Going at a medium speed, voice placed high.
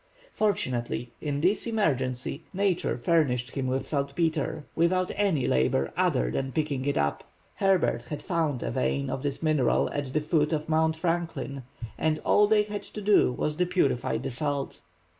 No: average, 165 wpm; medium, 150 Hz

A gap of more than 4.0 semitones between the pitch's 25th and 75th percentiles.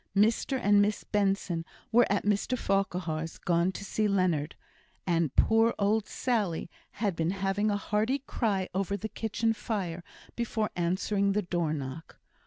No: average, 3.6 semitones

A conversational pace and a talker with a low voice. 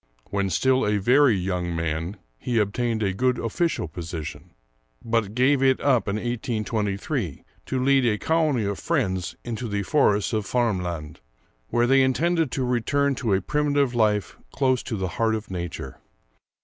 Yes: average, 160 wpm; low, 115 Hz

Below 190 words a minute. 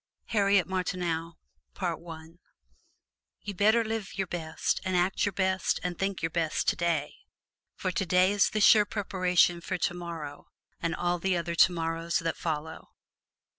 Yes: slow, 135 wpm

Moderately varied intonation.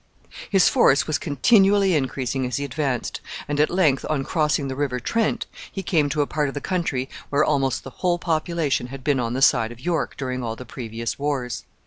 Yes: average, 3.7 semitones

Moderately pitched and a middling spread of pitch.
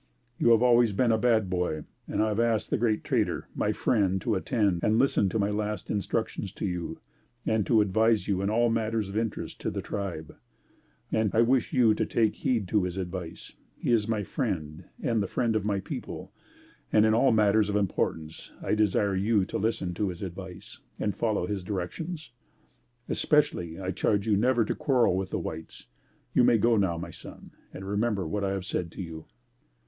No: low, 105 Hz; average, 3.2 semitones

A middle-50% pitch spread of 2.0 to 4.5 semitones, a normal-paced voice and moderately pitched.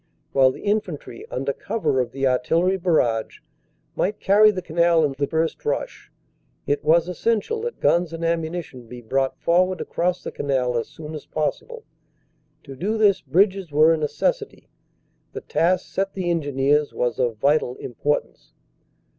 No: average, 5.2 semitones; average, 155 wpm; medium, 160 Hz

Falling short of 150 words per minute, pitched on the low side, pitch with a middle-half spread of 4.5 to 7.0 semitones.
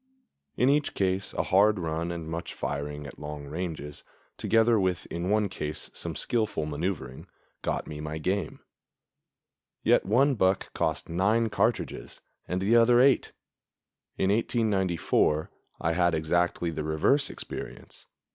Yes: slow, 135 wpm; very low, 90 Hz; wide, 5.5 semitones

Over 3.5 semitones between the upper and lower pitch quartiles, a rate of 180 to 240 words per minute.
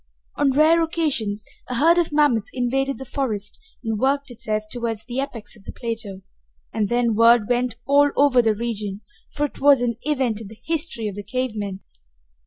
Yes: average, 4.4 semitones; average, 190 wpm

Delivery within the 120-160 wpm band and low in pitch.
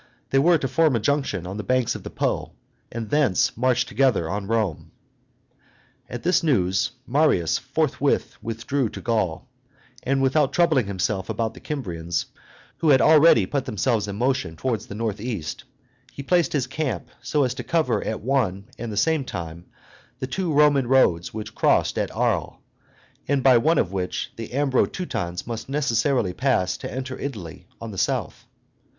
No: average, 170 wpm; low, 125 Hz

